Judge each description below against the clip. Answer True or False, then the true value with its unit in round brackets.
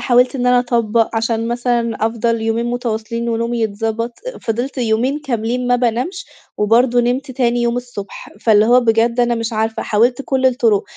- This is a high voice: True (235 Hz)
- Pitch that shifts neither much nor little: False (1.5 semitones)